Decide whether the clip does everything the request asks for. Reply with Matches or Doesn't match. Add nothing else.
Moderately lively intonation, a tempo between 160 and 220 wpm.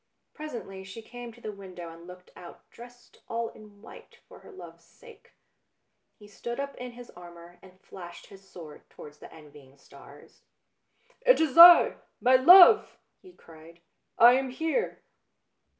Doesn't match